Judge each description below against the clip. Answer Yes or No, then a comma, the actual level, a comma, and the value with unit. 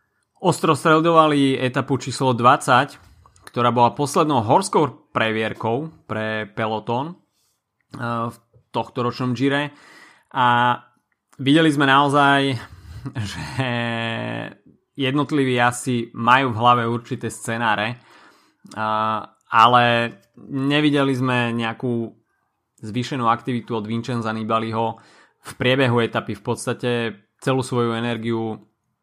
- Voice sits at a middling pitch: No, low, 120 Hz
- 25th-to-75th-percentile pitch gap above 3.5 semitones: No, average, 2.8 semitones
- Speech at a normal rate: No, slow, 90 wpm